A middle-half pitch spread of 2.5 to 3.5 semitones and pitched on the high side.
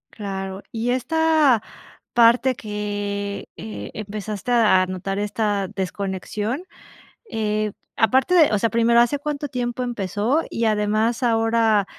Yes: average, 2.9 semitones; high, 220 Hz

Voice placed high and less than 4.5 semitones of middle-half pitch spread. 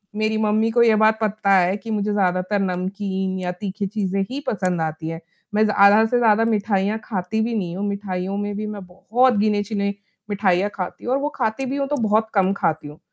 Yes: high, 205 Hz; narrow, 2.6 semitones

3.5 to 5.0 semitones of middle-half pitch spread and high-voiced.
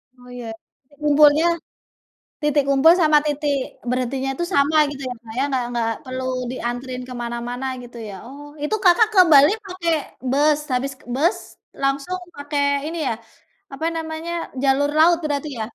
No: average, 3.1 semitones; very high, 280 Hz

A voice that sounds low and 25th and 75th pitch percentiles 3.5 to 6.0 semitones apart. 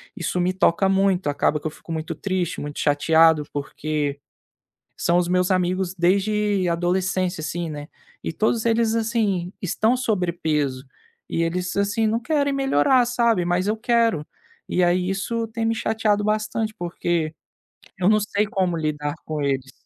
No: medium, 185 Hz; average, 4.8 semitones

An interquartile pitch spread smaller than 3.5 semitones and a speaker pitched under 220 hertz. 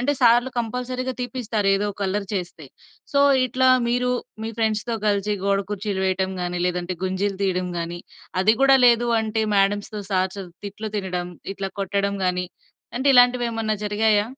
No: average, 3.9 semitones; high, 205 Hz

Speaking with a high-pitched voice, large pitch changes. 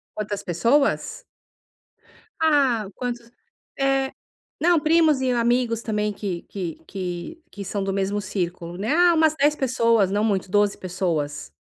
Yes: high, 220 Hz; wide, 5.9 semitones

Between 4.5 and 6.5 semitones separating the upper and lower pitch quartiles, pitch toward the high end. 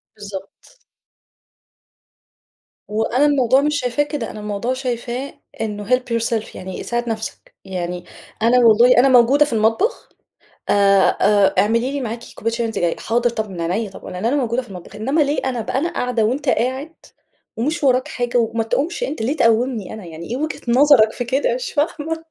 No: average, 3.8 semitones; high, 240 Hz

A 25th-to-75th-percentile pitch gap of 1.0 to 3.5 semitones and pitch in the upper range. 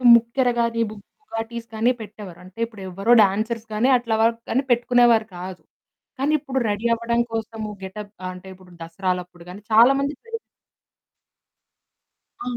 Yes: average, 3.2 semitones; high, 225 Hz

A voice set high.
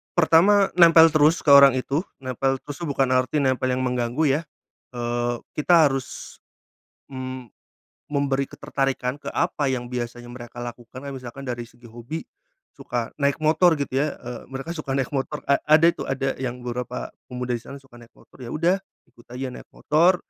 No: low, 135 Hz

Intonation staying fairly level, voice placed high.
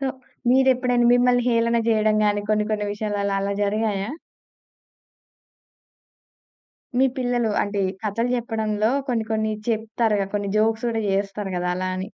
Yes: narrow, 2.3 semitones; high, 220 Hz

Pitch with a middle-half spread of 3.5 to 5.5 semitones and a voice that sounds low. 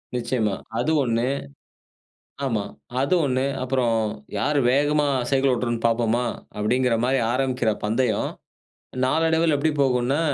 No: average, 2.8 semitones; low, 130 Hz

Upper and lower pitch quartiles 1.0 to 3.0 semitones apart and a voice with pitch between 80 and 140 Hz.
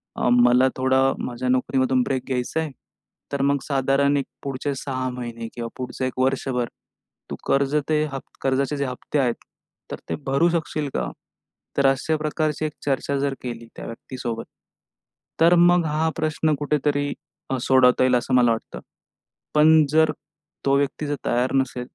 Yes: average, 2.7 semitones; low, 135 Hz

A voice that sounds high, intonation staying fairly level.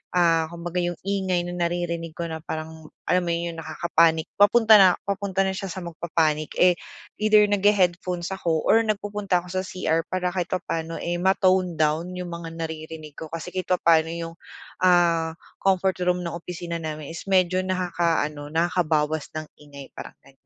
No: medium, 170 Hz; narrow, 2.3 semitones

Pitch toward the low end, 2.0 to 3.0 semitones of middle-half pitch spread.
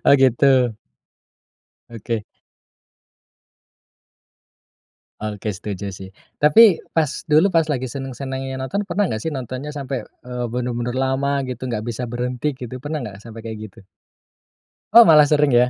No: low, 130 Hz; average, 3.9 semitones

